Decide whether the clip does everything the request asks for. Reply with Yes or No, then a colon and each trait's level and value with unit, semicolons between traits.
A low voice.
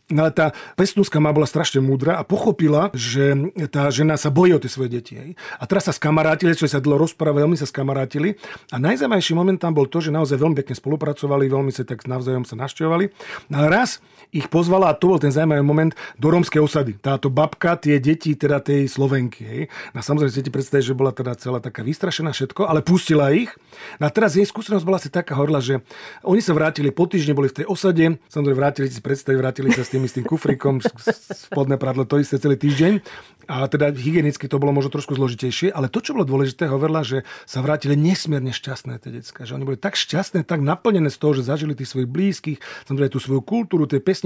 No: medium, 145 Hz